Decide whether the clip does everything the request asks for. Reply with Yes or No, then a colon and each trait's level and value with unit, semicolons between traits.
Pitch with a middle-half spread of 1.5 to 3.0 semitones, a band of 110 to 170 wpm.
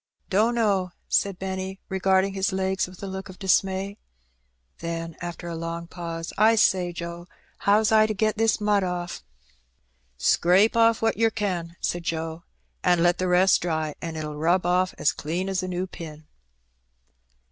Yes: narrow, 2.6 semitones; average, 165 wpm